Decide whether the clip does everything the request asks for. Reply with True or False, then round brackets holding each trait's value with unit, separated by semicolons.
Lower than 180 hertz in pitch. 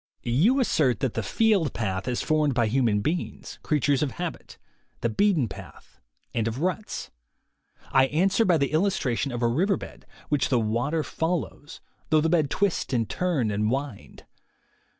True (140 Hz)